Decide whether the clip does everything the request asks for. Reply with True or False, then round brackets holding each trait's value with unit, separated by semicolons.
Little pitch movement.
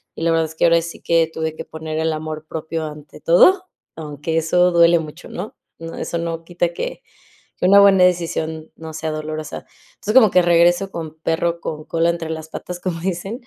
True (1.8 semitones)